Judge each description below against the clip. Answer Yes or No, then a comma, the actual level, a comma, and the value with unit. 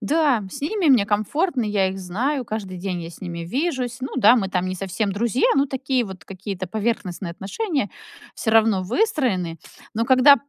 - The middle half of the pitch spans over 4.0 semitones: Yes, wide, 5.6 semitones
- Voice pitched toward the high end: Yes, high, 215 Hz